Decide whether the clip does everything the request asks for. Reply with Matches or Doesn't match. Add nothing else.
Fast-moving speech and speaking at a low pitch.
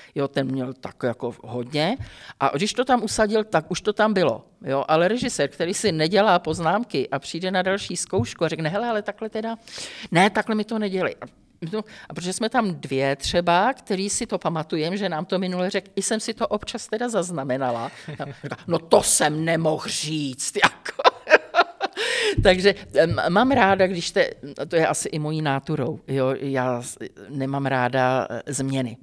Doesn't match